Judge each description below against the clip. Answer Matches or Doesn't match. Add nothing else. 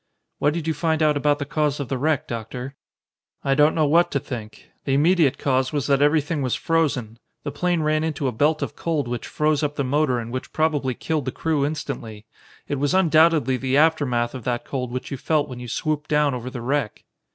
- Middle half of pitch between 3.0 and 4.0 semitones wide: Matches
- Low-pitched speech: Doesn't match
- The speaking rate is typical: Doesn't match